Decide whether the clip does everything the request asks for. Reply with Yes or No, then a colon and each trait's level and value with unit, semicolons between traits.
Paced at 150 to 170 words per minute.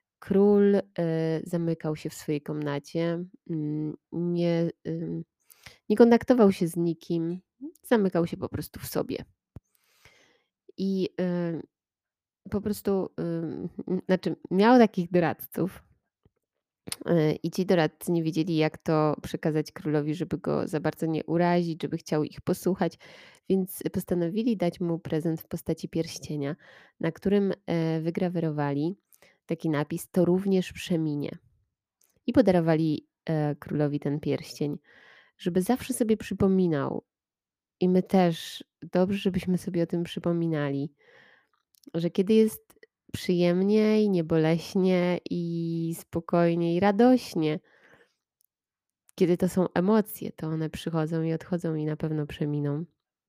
No: average, 115 wpm